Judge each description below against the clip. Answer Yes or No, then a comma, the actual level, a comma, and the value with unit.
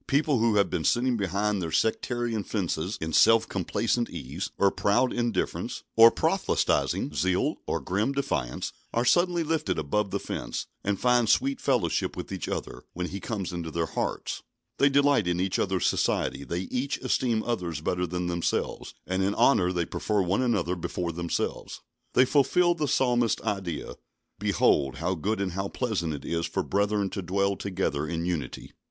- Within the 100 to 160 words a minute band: No, average, 170 wpm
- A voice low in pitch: Yes, low, 100 Hz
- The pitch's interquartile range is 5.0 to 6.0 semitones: Yes, wide, 5.4 semitones